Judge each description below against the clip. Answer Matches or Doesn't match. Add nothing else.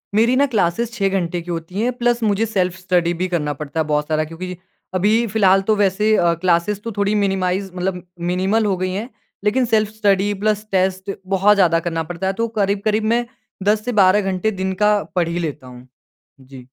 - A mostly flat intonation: Doesn't match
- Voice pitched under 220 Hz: Matches